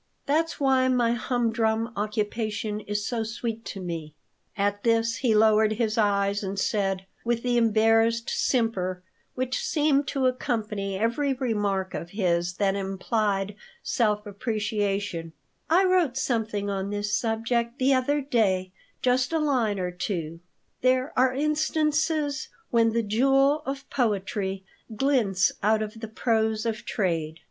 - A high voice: Yes, high, 220 Hz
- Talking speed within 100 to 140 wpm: Yes, slow, 135 wpm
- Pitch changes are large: No, average, 3.9 semitones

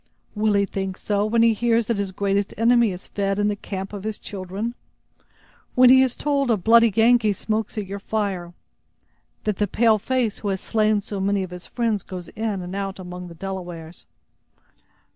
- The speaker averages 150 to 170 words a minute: No, average, 195 wpm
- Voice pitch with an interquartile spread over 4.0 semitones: No, average, 2.8 semitones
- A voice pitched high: Yes, high, 205 Hz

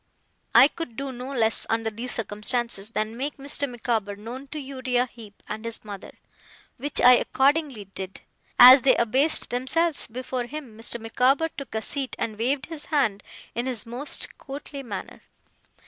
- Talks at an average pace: Yes, average, 160 wpm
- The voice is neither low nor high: No, very high, 250 Hz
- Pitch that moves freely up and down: No, average, 3.5 semitones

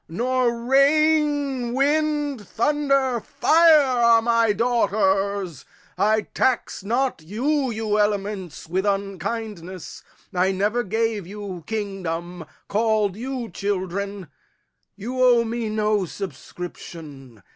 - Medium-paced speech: No, slow, 100 wpm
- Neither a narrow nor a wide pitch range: Yes, average, 4.6 semitones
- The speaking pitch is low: No, high, 215 Hz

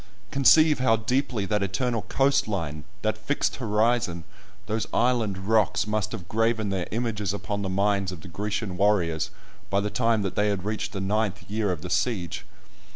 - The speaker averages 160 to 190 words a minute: Yes, average, 175 wpm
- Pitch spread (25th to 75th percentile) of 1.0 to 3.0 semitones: Yes, narrow, 2.6 semitones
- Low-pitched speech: Yes, low, 105 Hz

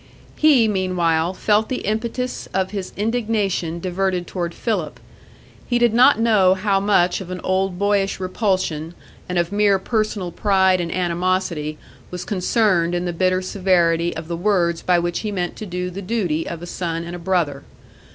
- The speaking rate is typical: Yes, average, 170 wpm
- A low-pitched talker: No, medium, 185 Hz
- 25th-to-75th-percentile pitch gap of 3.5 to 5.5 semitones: No, average, 2.9 semitones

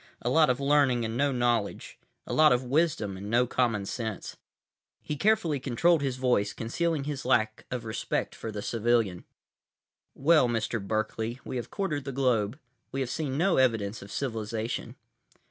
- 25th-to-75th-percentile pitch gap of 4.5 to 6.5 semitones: No, average, 4.0 semitones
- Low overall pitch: Yes, low, 125 Hz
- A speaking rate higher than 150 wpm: Yes, average, 165 wpm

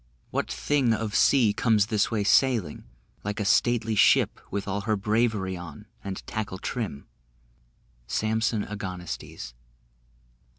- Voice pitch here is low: Yes, low, 105 Hz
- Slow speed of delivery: Yes, slow, 125 wpm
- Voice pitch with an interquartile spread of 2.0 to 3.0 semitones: Yes, narrow, 2.5 semitones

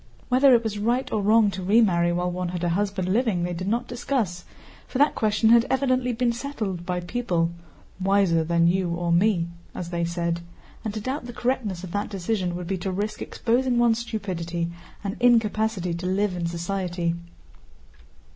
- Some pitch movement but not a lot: Yes, average, 4.8 semitones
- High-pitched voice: Yes, high, 195 Hz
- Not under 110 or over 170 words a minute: No, average, 185 wpm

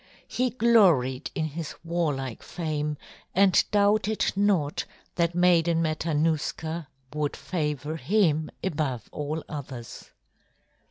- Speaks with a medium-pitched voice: Yes, medium, 160 Hz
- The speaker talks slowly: Yes, slow, 100 wpm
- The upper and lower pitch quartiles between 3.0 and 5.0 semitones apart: Yes, average, 3.3 semitones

